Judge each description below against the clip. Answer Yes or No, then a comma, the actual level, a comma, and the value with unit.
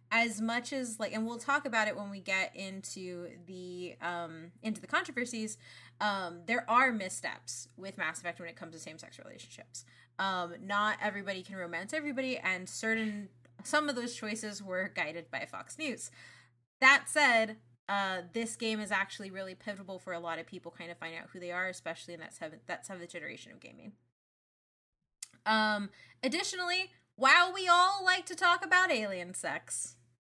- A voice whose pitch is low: No, high, 195 Hz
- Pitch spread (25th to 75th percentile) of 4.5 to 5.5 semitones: Yes, average, 5.2 semitones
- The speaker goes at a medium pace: Yes, average, 175 wpm